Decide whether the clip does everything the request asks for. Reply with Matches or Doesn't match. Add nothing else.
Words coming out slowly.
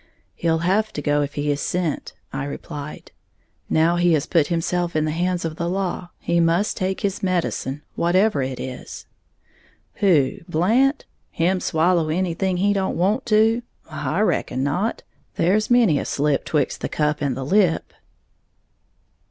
Doesn't match